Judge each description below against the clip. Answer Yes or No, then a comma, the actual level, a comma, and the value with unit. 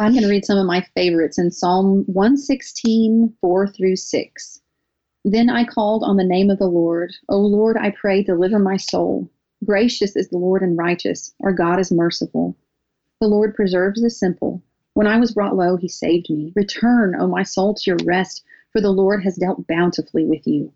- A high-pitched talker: Yes, high, 195 Hz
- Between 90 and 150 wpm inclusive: No, average, 195 wpm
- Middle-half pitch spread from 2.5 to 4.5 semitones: Yes, average, 2.9 semitones